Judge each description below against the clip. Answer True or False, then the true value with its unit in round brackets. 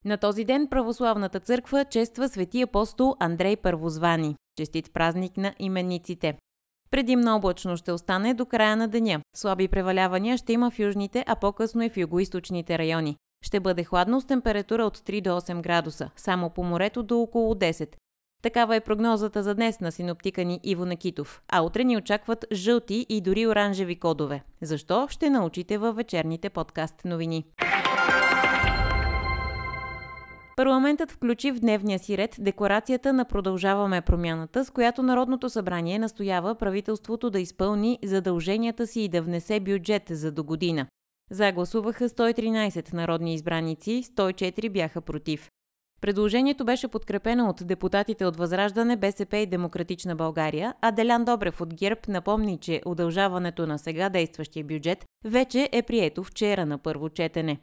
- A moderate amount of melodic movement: True (5.0 semitones)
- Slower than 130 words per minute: False (145 wpm)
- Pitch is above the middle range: True (195 Hz)